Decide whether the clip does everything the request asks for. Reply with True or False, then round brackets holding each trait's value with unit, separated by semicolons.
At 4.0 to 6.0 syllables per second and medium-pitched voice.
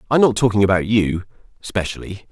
False (5.9 syllables/s; 105 Hz)